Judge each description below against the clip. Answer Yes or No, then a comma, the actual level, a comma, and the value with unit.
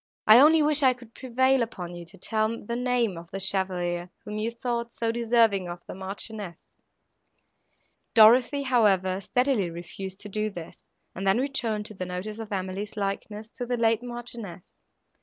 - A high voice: Yes, high, 215 Hz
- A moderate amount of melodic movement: Yes, average, 4.0 semitones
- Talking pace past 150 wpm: Yes, average, 170 wpm